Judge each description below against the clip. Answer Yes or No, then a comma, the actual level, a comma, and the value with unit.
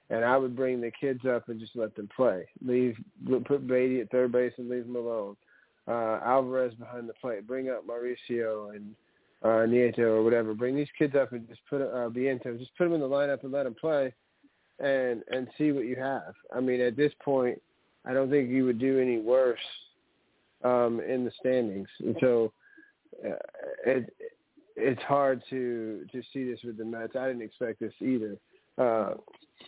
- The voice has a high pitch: No, low, 125 Hz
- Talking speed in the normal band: Yes, average, 190 wpm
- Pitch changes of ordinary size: No, narrow, 2.3 semitones